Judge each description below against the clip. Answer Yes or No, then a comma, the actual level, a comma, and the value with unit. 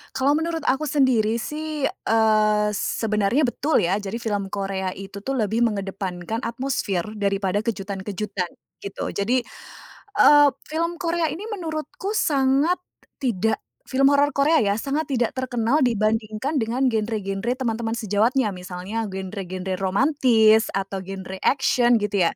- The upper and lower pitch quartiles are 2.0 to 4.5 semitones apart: No, wide, 5.4 semitones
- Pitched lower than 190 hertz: No, high, 225 Hz